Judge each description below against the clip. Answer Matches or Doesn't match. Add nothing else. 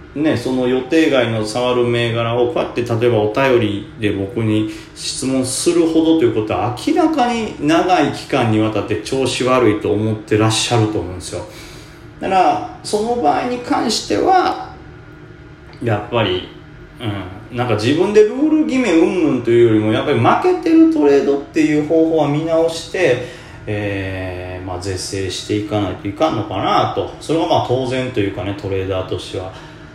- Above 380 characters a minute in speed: Doesn't match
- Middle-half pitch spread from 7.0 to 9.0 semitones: Matches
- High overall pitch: Doesn't match